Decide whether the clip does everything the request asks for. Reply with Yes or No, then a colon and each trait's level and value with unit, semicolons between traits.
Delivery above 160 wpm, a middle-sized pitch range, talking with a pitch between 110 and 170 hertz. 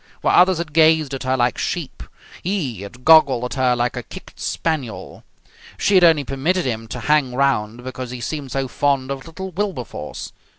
Yes: average, 185 wpm; average, 4.3 semitones; low, 135 Hz